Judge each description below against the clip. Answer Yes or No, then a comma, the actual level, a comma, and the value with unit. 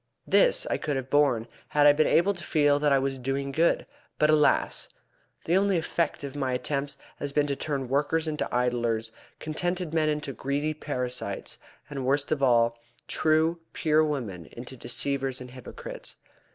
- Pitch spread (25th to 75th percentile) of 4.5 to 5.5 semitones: No, average, 3.0 semitones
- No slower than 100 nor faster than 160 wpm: No, average, 170 wpm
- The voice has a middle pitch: Yes, medium, 145 Hz